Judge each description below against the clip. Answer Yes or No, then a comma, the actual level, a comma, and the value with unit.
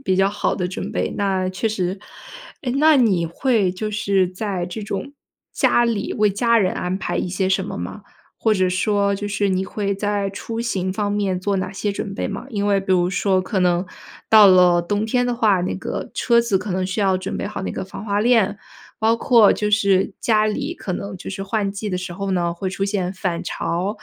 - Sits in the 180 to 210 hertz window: Yes, high, 200 Hz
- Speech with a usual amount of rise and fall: No, narrow, 2.3 semitones